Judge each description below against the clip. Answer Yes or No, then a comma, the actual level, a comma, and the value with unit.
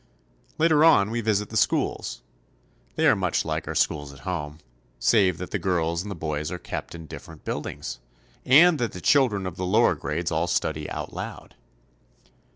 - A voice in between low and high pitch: No, very low, 90 Hz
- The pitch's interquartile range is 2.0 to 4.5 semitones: No, wide, 5.4 semitones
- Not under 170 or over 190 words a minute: Yes, average, 180 wpm